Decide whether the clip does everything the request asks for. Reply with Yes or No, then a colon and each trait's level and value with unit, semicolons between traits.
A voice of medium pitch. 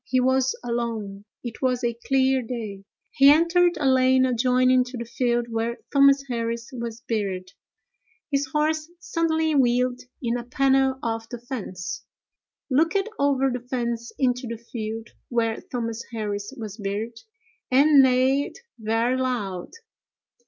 No: high, 245 Hz